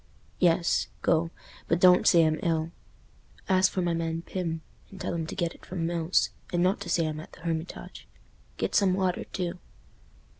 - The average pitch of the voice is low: No, medium, 170 Hz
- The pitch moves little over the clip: Yes, narrow, 1.8 semitones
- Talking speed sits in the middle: Yes, average, 180 wpm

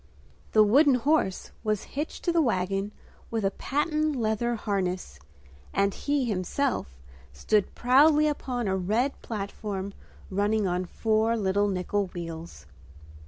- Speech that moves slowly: Yes, slow, 125 wpm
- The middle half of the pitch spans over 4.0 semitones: Yes, average, 5.1 semitones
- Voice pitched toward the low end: No, high, 215 Hz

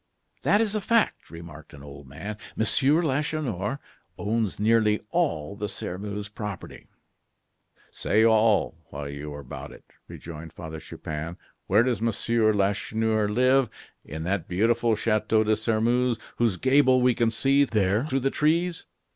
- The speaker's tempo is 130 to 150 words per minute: Yes, average, 145 wpm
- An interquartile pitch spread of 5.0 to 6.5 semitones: Yes, average, 5.3 semitones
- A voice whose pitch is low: Yes, low, 110 Hz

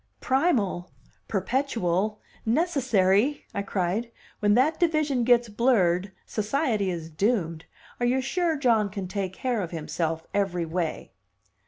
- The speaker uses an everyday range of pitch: No, wide, 5.9 semitones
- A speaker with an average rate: No, slow, 125 wpm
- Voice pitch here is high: Yes, high, 210 Hz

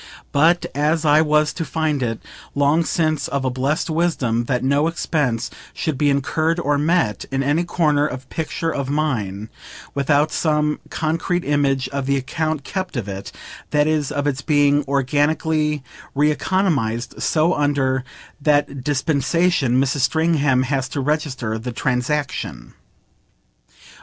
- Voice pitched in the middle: Yes, medium, 145 Hz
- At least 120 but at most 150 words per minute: Yes, average, 140 wpm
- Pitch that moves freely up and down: No, average, 2.9 semitones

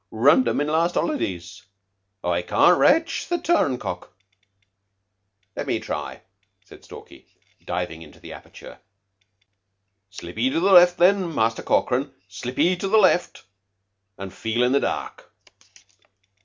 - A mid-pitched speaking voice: No, low, 130 Hz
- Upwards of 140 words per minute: No, slow, 135 wpm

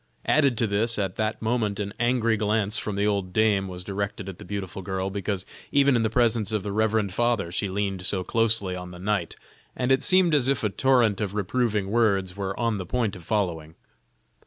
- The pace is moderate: No, fast, 210 wpm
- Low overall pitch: Yes, low, 105 Hz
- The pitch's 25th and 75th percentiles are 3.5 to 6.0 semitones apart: No, average, 2.9 semitones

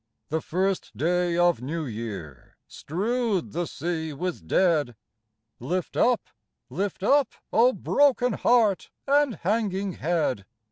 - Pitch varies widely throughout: Yes, wide, 5.7 semitones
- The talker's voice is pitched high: No, medium, 180 Hz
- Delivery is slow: Yes, slow, 120 wpm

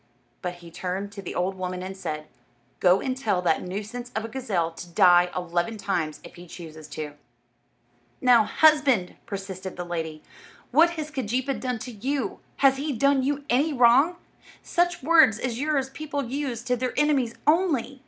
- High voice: Yes, high, 235 Hz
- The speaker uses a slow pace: No, average, 175 wpm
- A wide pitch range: Yes, wide, 7.2 semitones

